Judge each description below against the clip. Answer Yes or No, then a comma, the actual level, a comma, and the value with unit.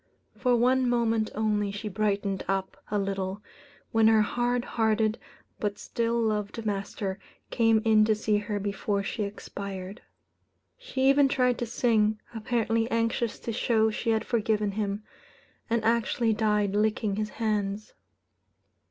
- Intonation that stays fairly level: Yes, narrow, 2.0 semitones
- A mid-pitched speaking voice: No, high, 215 Hz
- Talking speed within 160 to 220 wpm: No, average, 140 wpm